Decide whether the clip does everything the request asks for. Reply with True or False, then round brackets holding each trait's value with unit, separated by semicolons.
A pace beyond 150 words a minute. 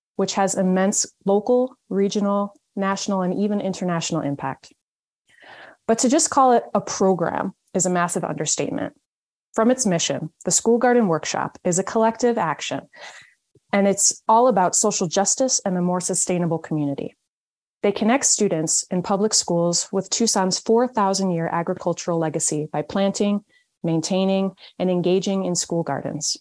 False (145 wpm)